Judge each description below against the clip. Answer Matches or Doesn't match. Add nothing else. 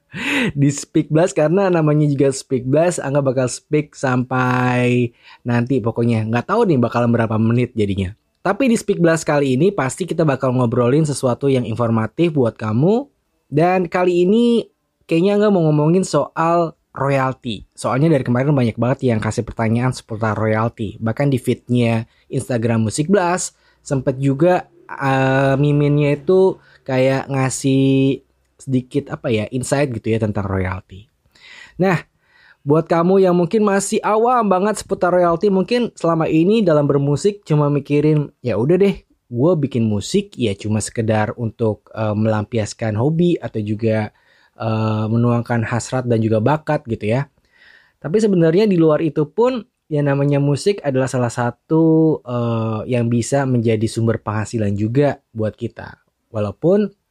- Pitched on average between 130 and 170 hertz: Matches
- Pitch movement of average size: Doesn't match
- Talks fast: Matches